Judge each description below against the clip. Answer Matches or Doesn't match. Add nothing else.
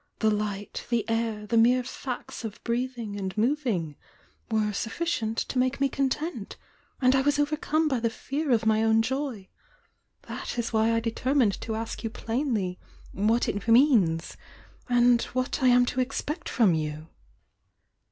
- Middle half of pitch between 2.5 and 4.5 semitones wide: Matches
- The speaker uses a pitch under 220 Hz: Doesn't match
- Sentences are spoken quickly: Doesn't match